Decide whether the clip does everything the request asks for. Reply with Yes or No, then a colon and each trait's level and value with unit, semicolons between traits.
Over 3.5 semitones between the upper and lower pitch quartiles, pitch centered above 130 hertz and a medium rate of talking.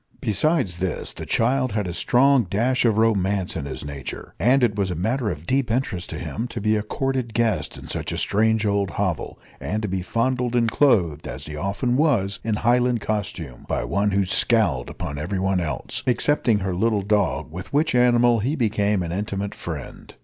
No: average, 4.4 semitones; low, 105 Hz; average, 195 wpm